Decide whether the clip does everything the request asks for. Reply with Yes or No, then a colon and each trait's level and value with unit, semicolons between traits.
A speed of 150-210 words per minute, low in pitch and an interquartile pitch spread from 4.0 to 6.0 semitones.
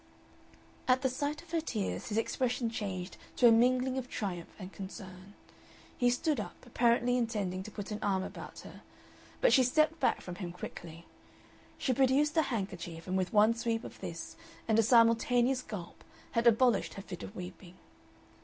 No: average, 175 wpm; high, 230 Hz; average, 4.9 semitones